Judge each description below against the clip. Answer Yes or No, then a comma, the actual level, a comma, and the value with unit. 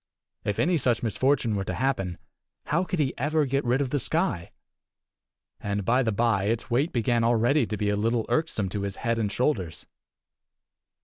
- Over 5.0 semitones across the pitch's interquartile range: No, average, 4.6 semitones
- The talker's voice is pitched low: Yes, low, 120 Hz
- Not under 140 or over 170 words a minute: No, average, 185 wpm